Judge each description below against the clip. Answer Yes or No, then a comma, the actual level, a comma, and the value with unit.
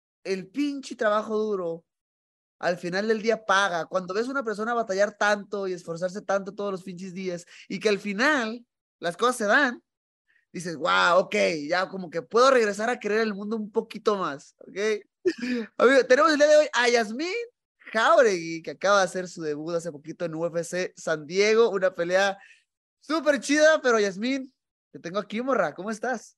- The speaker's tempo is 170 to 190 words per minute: Yes, average, 180 wpm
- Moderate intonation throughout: Yes, average, 4.7 semitones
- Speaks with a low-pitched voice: No, high, 210 Hz